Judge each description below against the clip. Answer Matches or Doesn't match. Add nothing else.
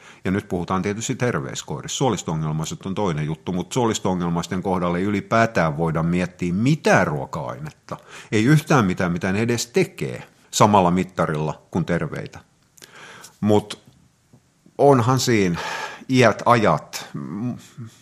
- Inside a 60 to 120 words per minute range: Matches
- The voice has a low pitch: Matches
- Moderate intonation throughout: Doesn't match